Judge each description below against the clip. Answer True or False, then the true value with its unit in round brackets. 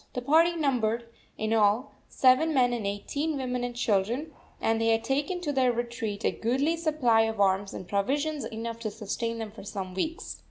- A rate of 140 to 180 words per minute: False (190 wpm)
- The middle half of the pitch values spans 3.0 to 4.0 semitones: False (4.4 semitones)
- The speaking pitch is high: True (235 Hz)